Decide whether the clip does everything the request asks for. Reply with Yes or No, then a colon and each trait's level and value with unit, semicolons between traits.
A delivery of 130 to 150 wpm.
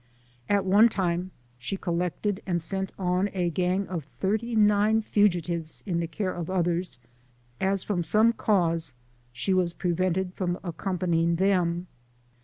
Yes: average, 140 wpm